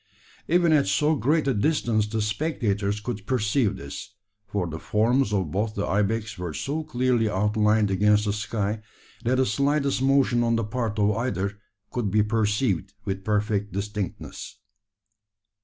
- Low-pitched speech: Yes, low, 105 Hz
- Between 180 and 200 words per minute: No, average, 155 wpm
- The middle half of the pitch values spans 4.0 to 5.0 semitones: No, average, 3.5 semitones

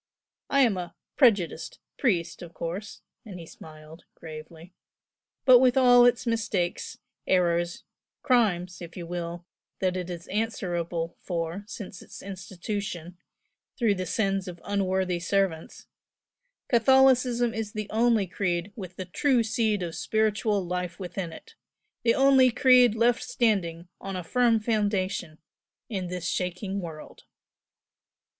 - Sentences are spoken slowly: Yes, slow, 130 wpm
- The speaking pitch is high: Yes, high, 195 Hz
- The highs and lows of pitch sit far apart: No, average, 4.7 semitones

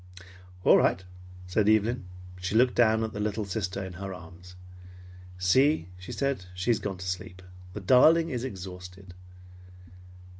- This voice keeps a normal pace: Yes, average, 150 wpm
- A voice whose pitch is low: Yes, low, 100 Hz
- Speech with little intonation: No, average, 3.8 semitones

